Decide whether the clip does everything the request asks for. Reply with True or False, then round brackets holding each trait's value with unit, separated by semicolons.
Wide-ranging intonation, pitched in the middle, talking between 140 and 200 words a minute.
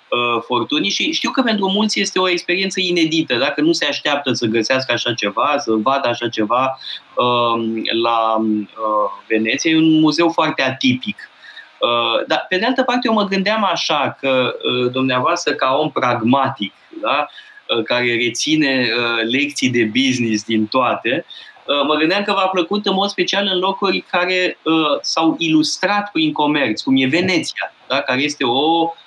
True (7.5 semitones; 145 Hz; 150 wpm)